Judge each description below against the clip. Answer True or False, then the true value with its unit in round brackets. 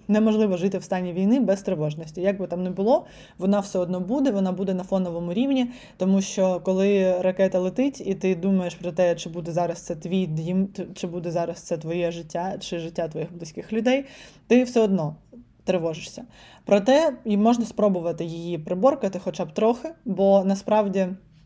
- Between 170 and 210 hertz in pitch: True (190 Hz)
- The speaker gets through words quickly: True (175 wpm)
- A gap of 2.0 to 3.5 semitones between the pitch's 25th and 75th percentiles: True (3.1 semitones)